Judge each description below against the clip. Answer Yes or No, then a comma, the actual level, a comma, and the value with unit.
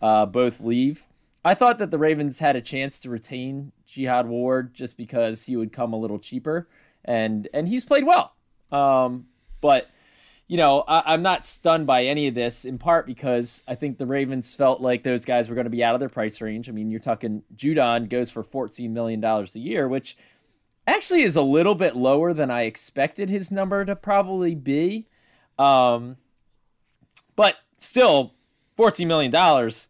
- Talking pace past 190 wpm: No, average, 185 wpm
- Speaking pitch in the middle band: No, low, 130 Hz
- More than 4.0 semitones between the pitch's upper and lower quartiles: Yes, average, 4.8 semitones